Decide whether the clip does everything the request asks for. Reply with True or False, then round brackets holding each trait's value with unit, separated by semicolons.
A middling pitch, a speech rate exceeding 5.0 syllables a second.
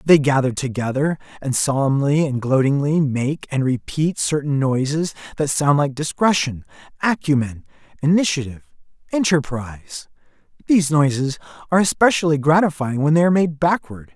True (145 Hz; 5.2 syllables/s)